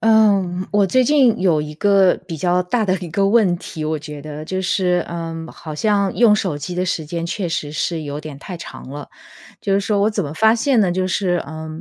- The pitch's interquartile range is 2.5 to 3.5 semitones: No, average, 4.1 semitones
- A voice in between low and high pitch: Yes, medium, 180 Hz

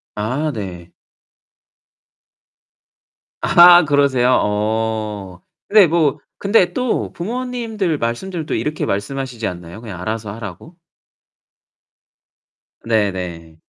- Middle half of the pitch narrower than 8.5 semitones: No, wide, 8.8 semitones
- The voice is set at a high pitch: No, low, 115 Hz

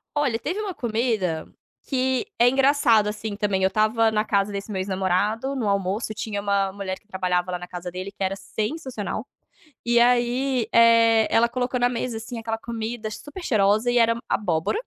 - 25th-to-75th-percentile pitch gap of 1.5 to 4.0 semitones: Yes, average, 3.4 semitones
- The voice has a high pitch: Yes, high, 220 Hz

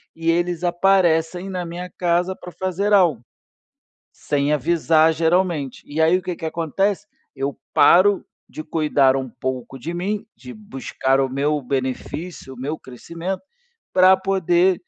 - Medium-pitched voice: Yes, medium, 170 Hz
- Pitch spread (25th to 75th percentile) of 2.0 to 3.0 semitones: No, average, 4.1 semitones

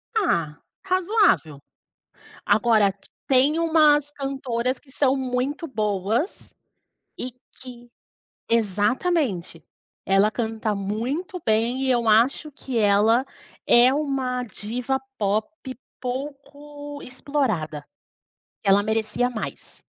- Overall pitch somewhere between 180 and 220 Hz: No, very high, 250 Hz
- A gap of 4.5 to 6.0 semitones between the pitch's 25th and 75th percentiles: Yes, average, 4.8 semitones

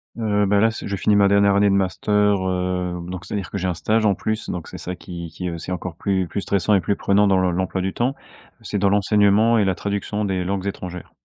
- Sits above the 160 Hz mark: No, low, 100 Hz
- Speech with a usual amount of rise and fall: No, narrow, 1.9 semitones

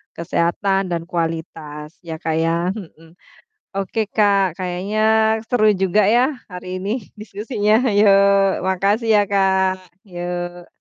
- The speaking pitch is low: No, high, 190 Hz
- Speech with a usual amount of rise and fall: Yes, average, 3.1 semitones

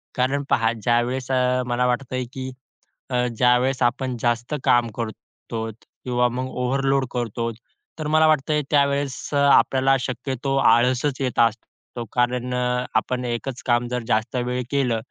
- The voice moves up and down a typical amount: No, narrow, 1.7 semitones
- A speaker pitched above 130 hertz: No, low, 125 Hz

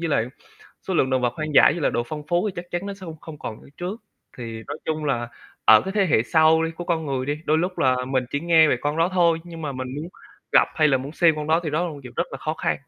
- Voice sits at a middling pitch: Yes, medium, 155 Hz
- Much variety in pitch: No, average, 3.9 semitones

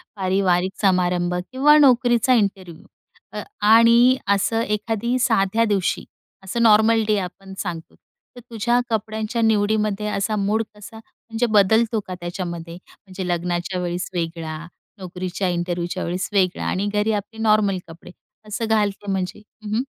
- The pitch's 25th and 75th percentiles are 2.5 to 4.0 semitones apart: Yes, average, 3.5 semitones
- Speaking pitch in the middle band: No, high, 205 Hz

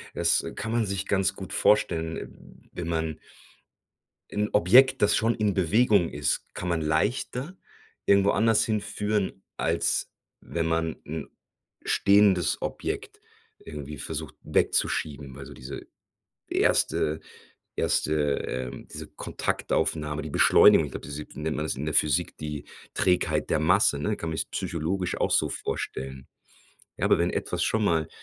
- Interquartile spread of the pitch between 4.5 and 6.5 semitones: Yes, average, 5.2 semitones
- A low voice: Yes, very low, 85 Hz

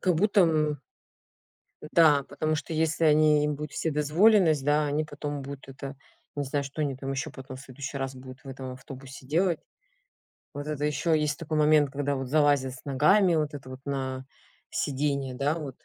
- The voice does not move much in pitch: Yes, narrow, 2.2 semitones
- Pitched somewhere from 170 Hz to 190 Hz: No, medium, 145 Hz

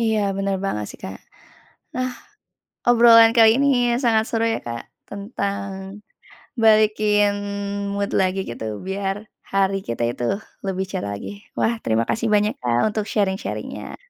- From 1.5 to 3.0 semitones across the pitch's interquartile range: Yes, narrow, 2.6 semitones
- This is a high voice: Yes, high, 200 Hz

